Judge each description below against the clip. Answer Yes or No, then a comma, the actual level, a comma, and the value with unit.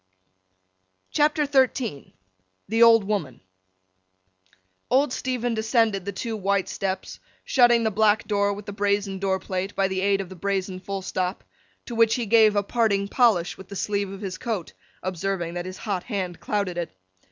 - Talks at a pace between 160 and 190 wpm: Yes, average, 170 wpm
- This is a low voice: No, high, 200 Hz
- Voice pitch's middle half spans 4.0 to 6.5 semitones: No, average, 3.0 semitones